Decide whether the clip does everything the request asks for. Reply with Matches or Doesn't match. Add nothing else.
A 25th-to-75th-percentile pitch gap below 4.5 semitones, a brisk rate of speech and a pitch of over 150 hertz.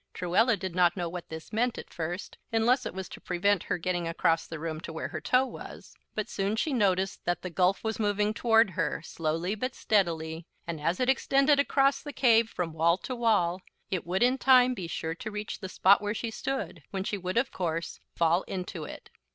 Doesn't match